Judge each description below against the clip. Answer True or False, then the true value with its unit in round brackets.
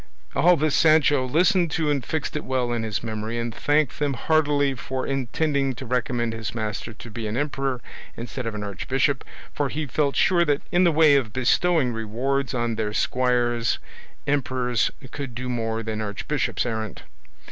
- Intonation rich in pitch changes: False (4.0 semitones)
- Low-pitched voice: True (130 Hz)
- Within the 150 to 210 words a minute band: True (175 wpm)